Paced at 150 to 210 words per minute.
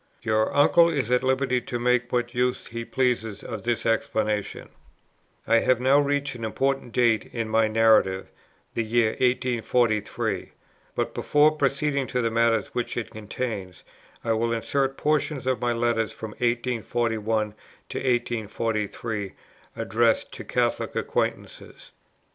No: slow, 135 wpm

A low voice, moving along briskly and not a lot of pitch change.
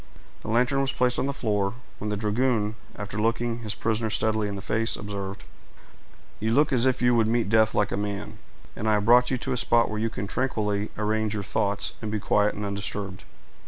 Yes: low, 110 Hz; fast, 220 wpm; narrow, 2.3 semitones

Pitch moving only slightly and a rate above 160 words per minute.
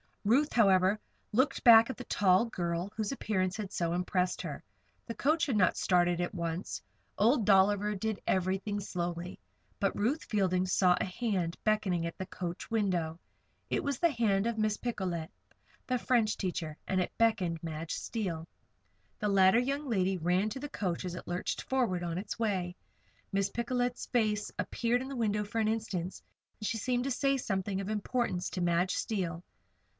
No: average, 4.2 semitones; average, 180 wpm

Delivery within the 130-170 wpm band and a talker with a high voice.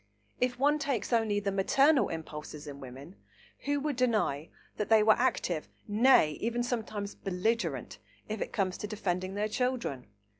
Yes: average, 155 wpm; high, 210 Hz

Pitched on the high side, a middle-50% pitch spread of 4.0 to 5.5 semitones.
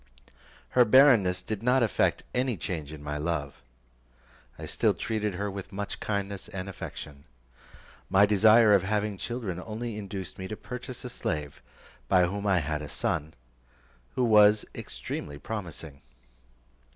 No: low, 100 Hz; average, 4.4 semitones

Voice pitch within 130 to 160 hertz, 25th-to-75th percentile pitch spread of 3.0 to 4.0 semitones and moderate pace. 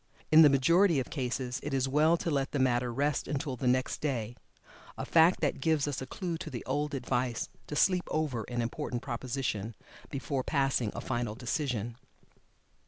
Yes: low, 135 Hz; average, 3.4 semitones; average, 180 wpm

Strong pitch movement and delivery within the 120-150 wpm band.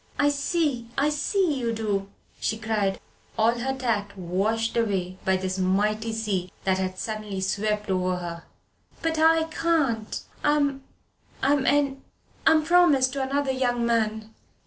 Yes: wide, 6.0 semitones; average, 145 wpm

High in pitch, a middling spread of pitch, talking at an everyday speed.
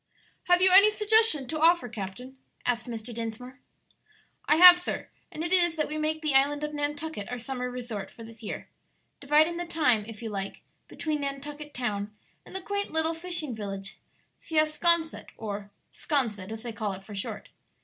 No: very high, 280 Hz; wide, 6.2 semitones; average, 180 wpm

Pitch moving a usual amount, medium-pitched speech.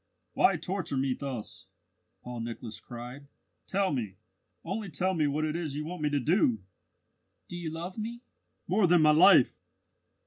No: wide, 5.9 semitones; medium, 155 Hz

